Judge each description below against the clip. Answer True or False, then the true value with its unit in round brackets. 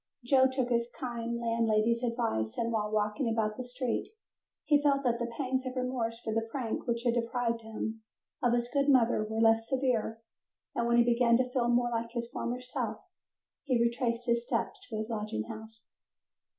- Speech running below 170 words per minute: False (190 wpm)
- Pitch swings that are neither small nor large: False (1.8 semitones)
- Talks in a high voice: True (235 Hz)